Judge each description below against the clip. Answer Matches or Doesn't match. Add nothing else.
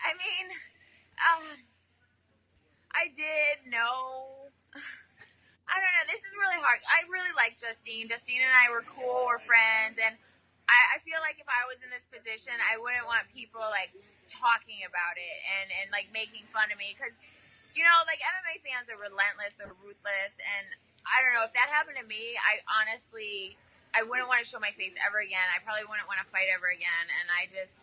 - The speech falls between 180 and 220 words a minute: Matches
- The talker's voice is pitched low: Doesn't match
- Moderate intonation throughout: Doesn't match